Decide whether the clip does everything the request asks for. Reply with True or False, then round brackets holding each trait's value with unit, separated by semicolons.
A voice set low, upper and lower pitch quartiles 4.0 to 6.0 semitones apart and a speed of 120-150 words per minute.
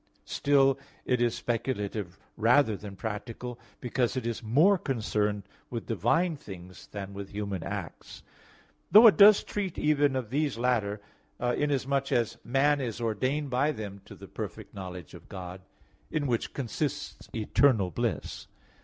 True (120 Hz; 5.3 semitones; 145 wpm)